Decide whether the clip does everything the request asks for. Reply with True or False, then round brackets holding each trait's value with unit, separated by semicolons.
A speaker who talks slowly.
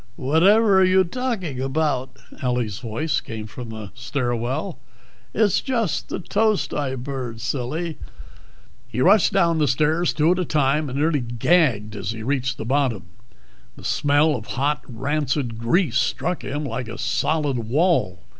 False (155 wpm)